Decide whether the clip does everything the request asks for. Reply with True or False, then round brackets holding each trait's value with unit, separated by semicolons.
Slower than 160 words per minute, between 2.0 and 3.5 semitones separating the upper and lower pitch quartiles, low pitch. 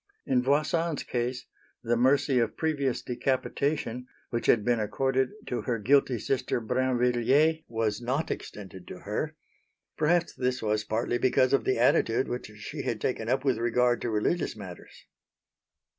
True (150 wpm; 2.8 semitones; 125 Hz)